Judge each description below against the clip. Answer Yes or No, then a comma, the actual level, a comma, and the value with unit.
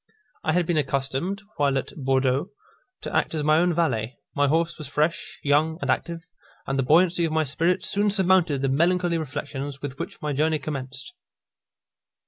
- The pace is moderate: Yes, average, 175 wpm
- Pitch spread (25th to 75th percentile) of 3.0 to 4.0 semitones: Yes, average, 3.7 semitones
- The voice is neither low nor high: Yes, medium, 155 Hz